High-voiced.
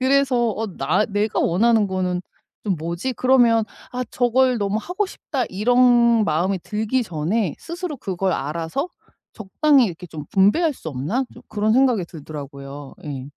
Yes: high, 210 Hz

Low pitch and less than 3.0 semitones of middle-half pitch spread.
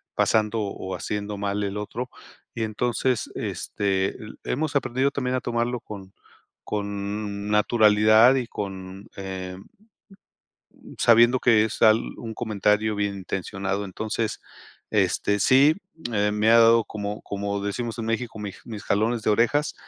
Yes: low, 105 Hz; narrow, 2.4 semitones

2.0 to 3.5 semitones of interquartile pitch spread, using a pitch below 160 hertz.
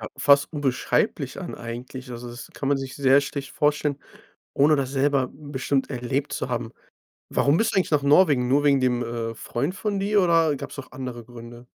Yes: average, 2.8 semitones; low, 135 Hz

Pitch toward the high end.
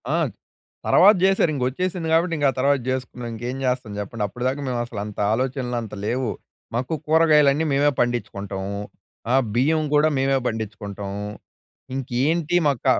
No: low, 130 Hz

